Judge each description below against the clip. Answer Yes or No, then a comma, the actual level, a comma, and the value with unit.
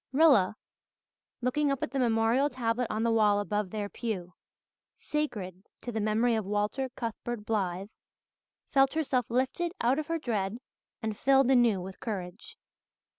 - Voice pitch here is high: Yes, high, 230 Hz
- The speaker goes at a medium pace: Yes, average, 150 wpm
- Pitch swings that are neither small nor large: Yes, average, 4.2 semitones